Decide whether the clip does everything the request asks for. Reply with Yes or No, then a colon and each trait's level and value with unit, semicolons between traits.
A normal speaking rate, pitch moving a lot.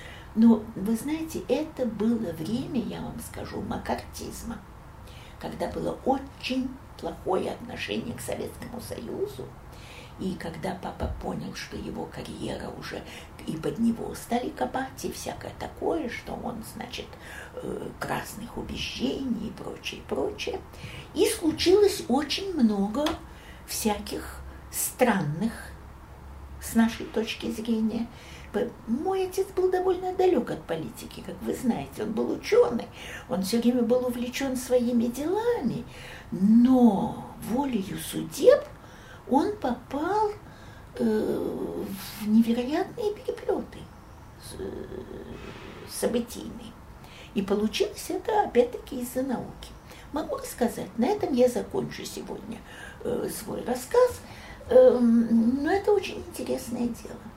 No: slow, 105 wpm; wide, 8.6 semitones